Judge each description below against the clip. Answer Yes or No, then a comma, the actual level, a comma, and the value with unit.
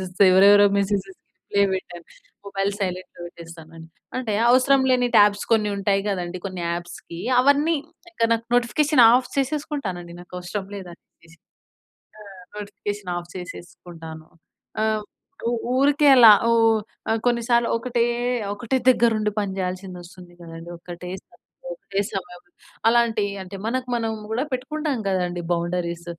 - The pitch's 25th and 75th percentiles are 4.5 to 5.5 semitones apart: Yes, average, 5.1 semitones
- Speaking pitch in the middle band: No, high, 200 Hz